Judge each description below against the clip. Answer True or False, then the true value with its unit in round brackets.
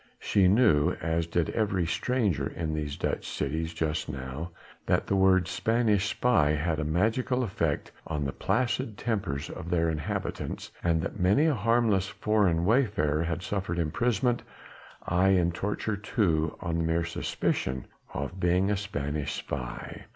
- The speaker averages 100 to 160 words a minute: True (150 wpm)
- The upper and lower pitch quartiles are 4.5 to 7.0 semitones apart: True (4.9 semitones)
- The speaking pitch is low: True (90 Hz)